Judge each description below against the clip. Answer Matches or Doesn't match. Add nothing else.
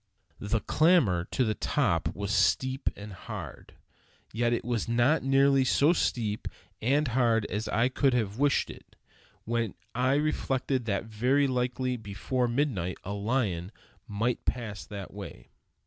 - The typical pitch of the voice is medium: Doesn't match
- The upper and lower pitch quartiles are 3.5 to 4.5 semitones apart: Matches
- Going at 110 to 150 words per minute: Matches